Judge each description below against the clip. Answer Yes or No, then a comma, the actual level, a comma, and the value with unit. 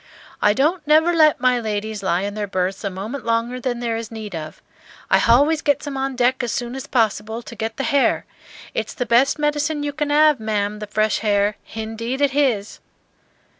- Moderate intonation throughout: Yes, average, 4.8 semitones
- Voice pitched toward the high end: Yes, high, 235 Hz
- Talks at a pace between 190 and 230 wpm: Yes, fast, 205 wpm